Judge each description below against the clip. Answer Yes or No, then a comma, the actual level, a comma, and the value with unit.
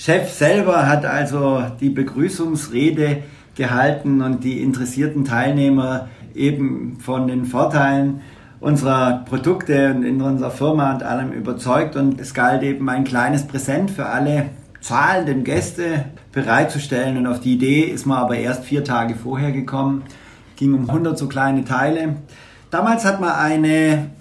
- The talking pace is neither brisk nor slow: Yes, average, 145 wpm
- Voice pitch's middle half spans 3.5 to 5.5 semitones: No, narrow, 2.4 semitones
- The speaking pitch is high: No, low, 135 Hz